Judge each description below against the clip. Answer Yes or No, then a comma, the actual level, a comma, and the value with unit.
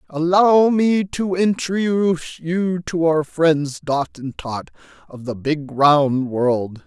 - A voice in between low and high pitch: Yes, medium, 160 Hz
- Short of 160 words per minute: Yes, average, 140 wpm